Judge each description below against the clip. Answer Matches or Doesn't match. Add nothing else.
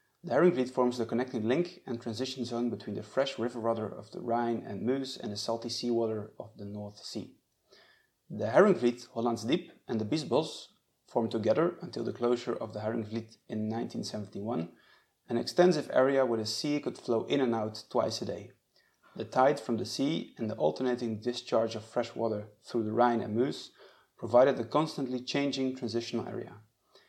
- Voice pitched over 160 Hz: Doesn't match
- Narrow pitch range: Matches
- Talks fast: Doesn't match